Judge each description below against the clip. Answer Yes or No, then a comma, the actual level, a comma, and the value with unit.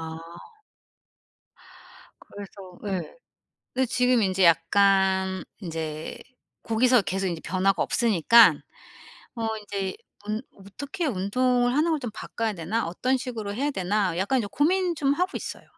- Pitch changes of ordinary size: Yes, average, 5.0 semitones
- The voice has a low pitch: No, high, 210 Hz